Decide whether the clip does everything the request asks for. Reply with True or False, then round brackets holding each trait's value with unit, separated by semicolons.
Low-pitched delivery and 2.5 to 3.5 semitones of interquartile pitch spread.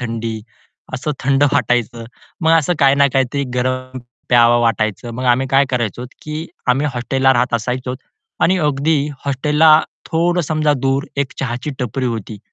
True (130 Hz; 2.9 semitones)